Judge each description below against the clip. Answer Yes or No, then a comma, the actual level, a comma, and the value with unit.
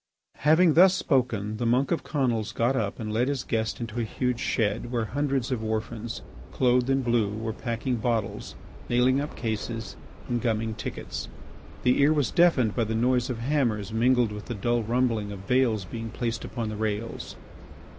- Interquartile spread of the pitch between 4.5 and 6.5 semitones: No, average, 2.7 semitones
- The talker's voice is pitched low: Yes, low, 120 Hz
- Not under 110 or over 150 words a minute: No, average, 180 wpm